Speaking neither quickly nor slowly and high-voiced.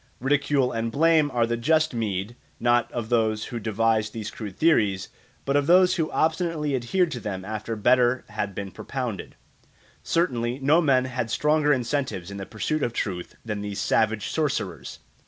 No: average, 175 wpm; low, 120 Hz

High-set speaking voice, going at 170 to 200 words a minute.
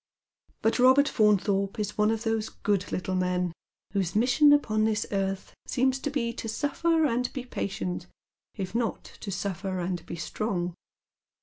No: high, 215 Hz; average, 160 wpm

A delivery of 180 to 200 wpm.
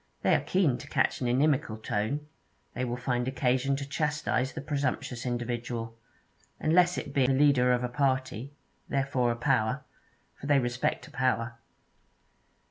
No: average, 155 wpm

